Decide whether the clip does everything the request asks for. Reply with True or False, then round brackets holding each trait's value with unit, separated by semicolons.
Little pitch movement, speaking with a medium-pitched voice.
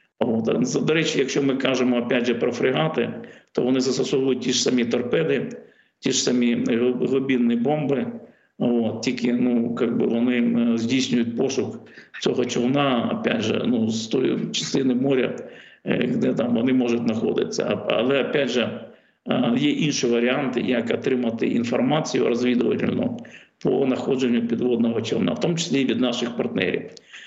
False (1.7 semitones; 125 Hz)